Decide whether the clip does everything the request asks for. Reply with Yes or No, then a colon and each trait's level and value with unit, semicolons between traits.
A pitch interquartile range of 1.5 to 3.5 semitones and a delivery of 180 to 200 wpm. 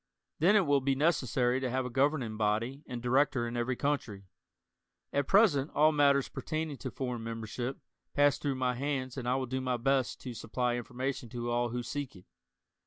Yes: average, 2.7 semitones; average, 190 wpm